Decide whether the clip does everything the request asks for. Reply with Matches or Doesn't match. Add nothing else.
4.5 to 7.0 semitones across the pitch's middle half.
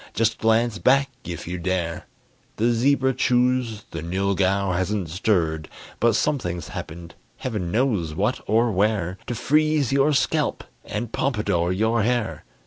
Matches